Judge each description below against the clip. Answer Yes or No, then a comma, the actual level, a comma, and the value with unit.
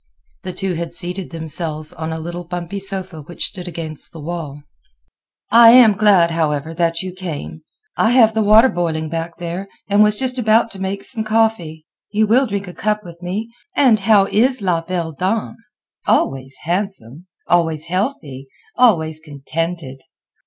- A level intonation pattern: No, average, 4.6 semitones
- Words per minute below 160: No, average, 165 wpm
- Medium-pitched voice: Yes, medium, 175 Hz